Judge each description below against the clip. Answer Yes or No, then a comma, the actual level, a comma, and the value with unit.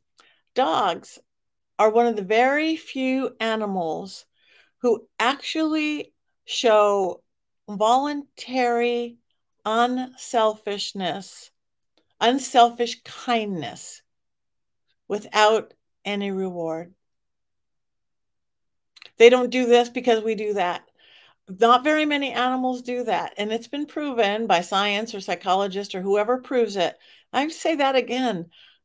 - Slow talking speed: Yes, slow, 100 wpm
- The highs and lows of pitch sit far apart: No, average, 3.8 semitones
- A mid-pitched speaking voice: No, high, 235 Hz